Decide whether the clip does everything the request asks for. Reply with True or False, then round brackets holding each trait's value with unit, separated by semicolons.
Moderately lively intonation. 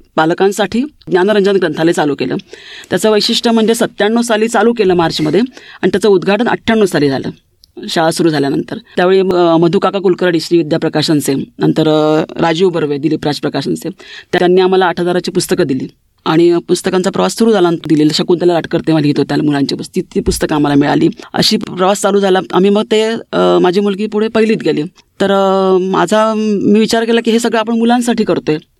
True (4.5 semitones)